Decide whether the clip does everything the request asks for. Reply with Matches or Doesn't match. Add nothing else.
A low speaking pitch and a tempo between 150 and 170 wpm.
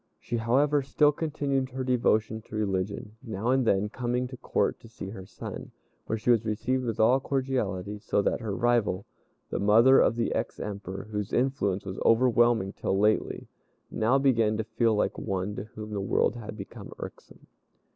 Doesn't match